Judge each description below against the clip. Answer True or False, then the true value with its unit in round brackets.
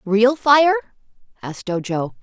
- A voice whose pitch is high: True (230 Hz)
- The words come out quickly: False (110 wpm)